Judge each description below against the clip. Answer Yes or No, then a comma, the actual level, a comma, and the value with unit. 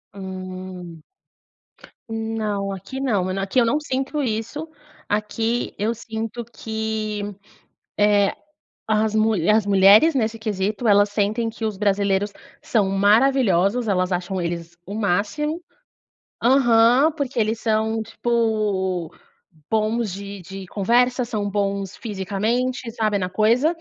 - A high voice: Yes, high, 215 Hz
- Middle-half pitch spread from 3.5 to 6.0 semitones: No, average, 2.8 semitones